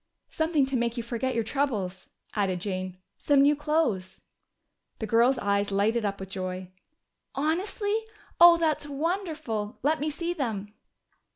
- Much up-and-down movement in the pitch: Yes, wide, 7.3 semitones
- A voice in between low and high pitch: No, high, 240 Hz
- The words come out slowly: No, average, 145 wpm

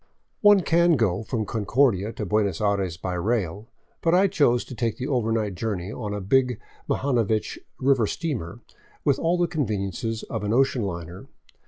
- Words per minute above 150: Yes, average, 170 wpm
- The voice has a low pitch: Yes, low, 115 Hz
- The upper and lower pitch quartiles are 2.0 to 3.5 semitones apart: No, average, 5.1 semitones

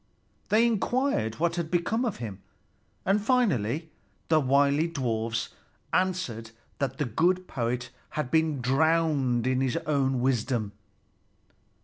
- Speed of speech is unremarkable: No, slow, 120 wpm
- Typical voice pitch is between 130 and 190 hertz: Yes, medium, 140 Hz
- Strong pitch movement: Yes, wide, 5.8 semitones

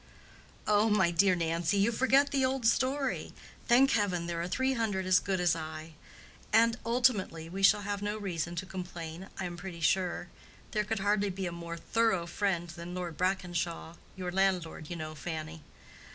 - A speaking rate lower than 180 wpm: Yes, average, 170 wpm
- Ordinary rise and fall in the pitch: Yes, average, 3.6 semitones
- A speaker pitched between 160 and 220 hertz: Yes, medium, 185 Hz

